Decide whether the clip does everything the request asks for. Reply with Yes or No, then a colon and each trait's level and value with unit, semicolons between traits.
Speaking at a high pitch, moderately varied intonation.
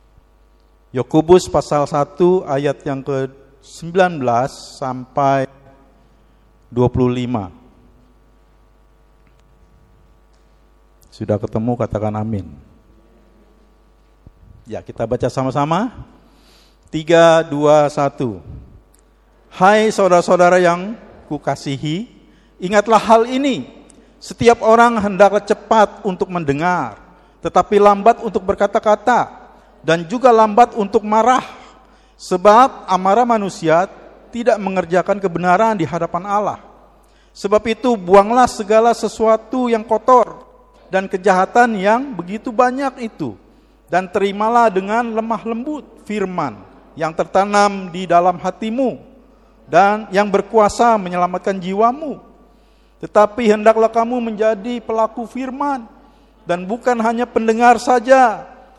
No: high, 200 Hz; wide, 6.4 semitones